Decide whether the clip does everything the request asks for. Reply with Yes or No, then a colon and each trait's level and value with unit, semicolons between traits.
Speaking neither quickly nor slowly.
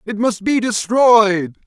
Yes: average, 145 wpm